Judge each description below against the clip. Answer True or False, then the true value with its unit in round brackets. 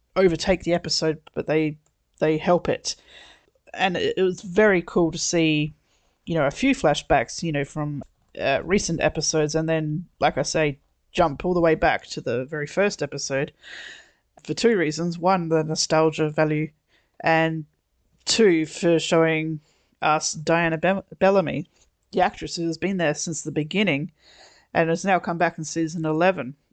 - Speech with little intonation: True (2.3 semitones)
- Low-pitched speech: False (160 Hz)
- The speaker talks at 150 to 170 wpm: True (160 wpm)